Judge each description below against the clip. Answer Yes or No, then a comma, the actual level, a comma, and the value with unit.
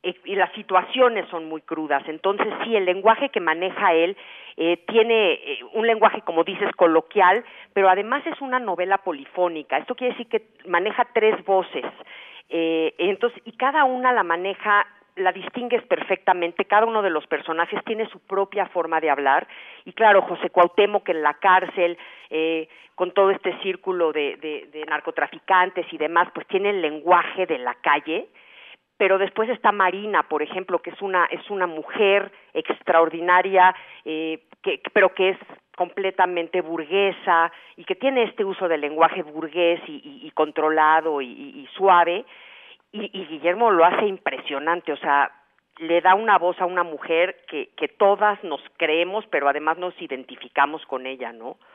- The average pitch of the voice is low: No, medium, 185 Hz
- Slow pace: No, average, 165 wpm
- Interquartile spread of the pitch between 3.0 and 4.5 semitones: Yes, average, 4.2 semitones